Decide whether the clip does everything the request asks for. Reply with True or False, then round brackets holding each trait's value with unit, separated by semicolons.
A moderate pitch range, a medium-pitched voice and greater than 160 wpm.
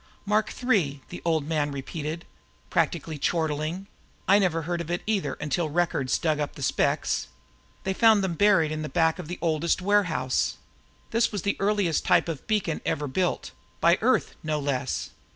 True (3.9 semitones; 165 Hz; 170 wpm)